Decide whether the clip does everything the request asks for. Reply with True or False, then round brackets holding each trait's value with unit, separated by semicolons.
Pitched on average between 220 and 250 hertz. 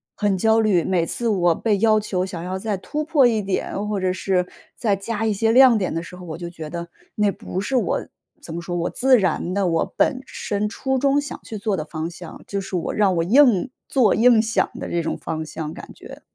False (200 Hz)